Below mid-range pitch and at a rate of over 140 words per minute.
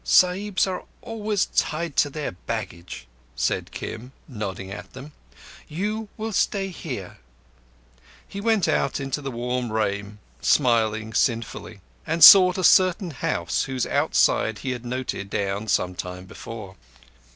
No: low, 130 Hz; slow, 135 wpm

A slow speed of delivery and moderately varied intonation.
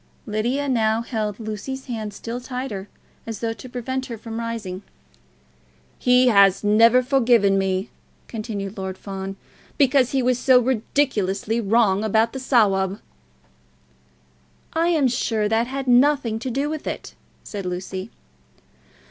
Yes: slow, 130 wpm; average, 3.7 semitones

